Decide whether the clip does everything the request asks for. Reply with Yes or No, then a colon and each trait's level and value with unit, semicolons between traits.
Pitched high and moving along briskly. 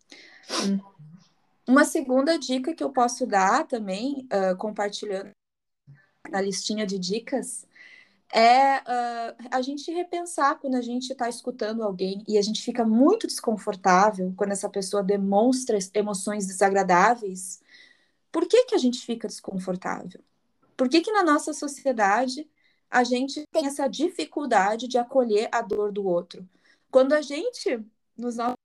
No: high, 235 Hz; average, 140 wpm